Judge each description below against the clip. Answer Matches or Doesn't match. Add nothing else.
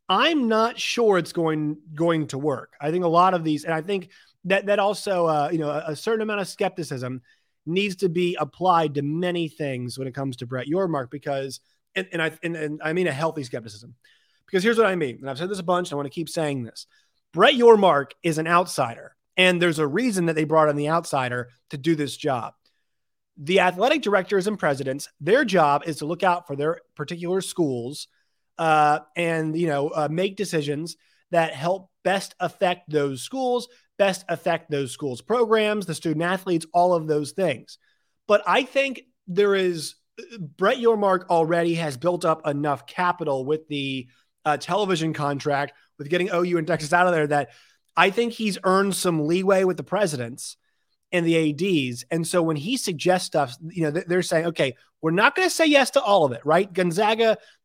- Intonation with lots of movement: Doesn't match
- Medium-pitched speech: Matches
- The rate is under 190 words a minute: Doesn't match